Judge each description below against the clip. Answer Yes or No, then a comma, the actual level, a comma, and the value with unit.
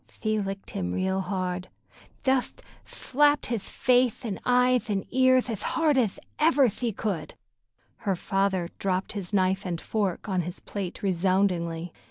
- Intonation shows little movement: No, average, 5.1 semitones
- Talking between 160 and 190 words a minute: No, average, 145 wpm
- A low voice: No, high, 195 Hz